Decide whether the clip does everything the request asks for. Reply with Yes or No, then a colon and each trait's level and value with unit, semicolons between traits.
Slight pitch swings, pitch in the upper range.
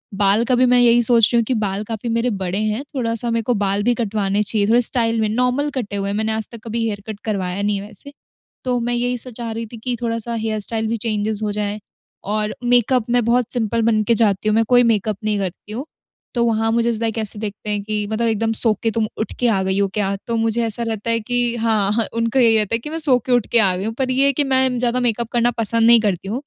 Yes: narrow, 2.2 semitones; high, 225 Hz